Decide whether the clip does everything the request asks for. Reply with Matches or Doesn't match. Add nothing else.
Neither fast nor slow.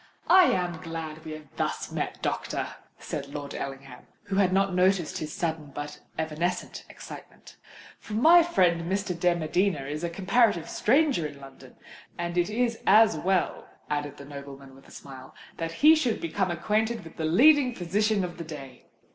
Matches